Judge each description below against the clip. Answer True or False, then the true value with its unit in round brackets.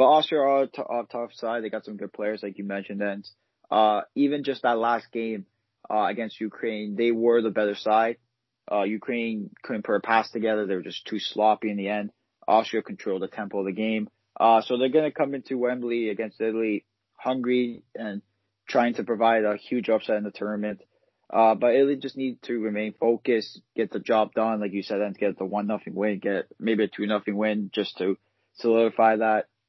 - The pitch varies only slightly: True (2.1 semitones)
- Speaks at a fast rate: True (210 wpm)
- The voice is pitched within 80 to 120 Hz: True (110 Hz)